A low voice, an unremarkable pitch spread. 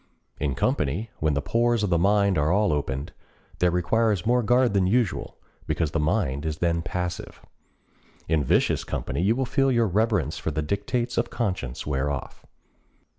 No: very low, 90 Hz; wide, 6.8 semitones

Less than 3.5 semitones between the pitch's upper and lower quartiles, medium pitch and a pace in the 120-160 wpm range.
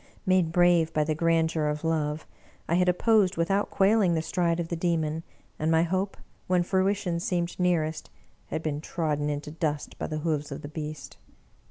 No: narrow, 2.5 semitones; medium, 165 Hz; average, 180 wpm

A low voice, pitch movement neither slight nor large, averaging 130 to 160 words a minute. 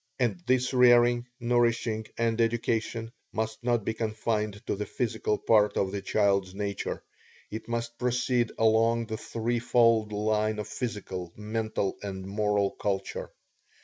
No: low, 110 Hz; narrow, 2.1 semitones; average, 140 wpm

